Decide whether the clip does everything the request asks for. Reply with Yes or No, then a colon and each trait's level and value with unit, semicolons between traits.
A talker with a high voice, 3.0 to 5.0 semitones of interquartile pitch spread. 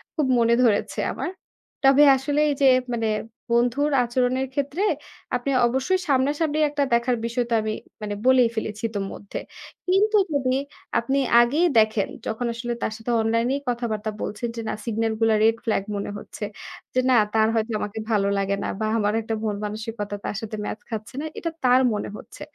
Yes: high, 235 Hz; average, 3.3 semitones